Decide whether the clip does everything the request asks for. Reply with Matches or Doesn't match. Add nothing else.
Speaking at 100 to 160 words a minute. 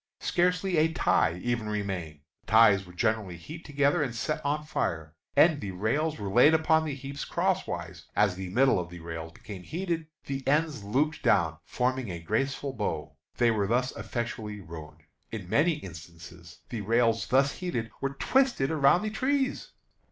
Doesn't match